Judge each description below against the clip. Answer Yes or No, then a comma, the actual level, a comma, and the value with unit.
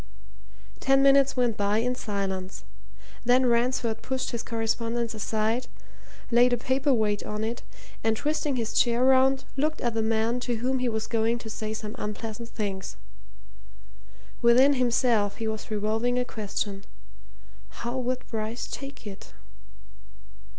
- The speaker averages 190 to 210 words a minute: No, average, 145 wpm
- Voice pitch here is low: No, high, 235 Hz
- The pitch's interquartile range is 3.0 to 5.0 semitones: No, narrow, 2.5 semitones